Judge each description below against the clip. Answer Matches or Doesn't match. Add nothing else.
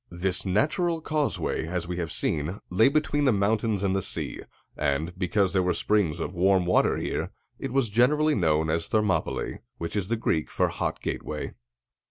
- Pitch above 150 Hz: Doesn't match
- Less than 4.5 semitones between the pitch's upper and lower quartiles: Doesn't match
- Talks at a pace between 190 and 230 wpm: Doesn't match